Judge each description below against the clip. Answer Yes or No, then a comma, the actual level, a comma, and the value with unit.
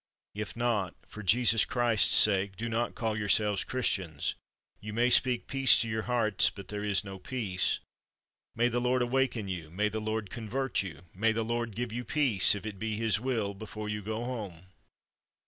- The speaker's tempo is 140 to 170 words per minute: No, average, 185 wpm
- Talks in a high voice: No, low, 110 Hz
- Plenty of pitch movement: No, average, 2.9 semitones